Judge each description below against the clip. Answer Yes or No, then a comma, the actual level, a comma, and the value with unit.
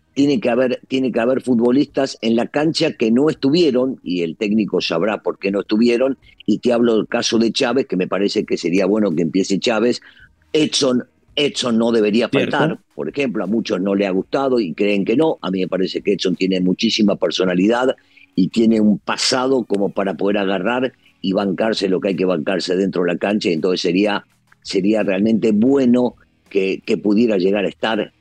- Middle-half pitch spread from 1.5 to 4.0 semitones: No, average, 4.4 semitones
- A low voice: Yes, low, 110 Hz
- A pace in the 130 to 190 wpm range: No, average, 200 wpm